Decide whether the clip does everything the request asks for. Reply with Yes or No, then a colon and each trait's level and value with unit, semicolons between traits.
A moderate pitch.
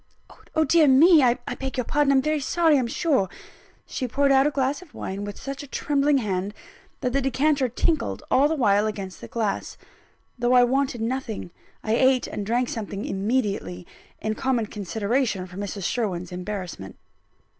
No: high, 245 Hz